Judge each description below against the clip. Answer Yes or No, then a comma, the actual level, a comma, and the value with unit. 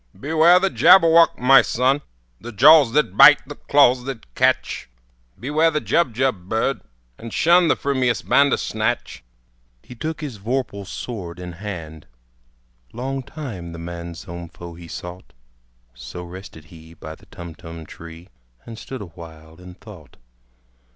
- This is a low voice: Yes, low, 110 Hz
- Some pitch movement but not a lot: No, wide, 8.2 semitones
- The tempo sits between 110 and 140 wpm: Yes, slow, 135 wpm